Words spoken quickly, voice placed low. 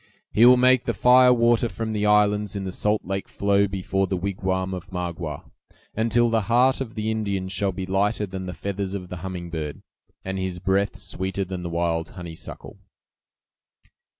No: average, 180 wpm; very low, 95 Hz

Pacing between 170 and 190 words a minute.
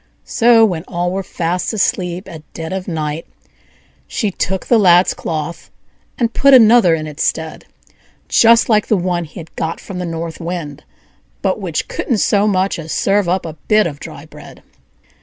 Yes: average, 175 wpm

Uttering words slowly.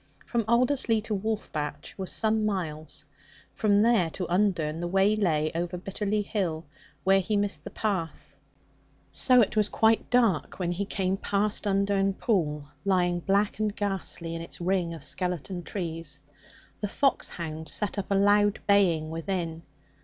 No: average, 155 wpm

